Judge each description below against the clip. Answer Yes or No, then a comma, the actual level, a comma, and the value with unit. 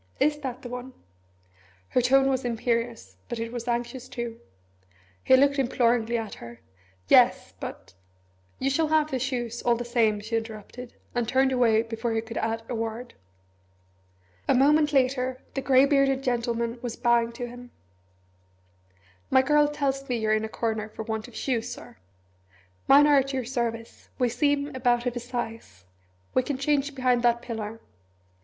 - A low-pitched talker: No, high, 245 Hz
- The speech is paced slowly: No, average, 170 wpm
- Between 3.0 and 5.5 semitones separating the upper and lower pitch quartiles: No, narrow, 2.6 semitones